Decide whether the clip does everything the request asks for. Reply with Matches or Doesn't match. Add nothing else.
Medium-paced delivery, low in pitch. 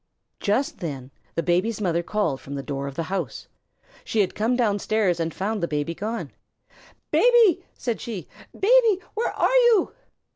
Doesn't match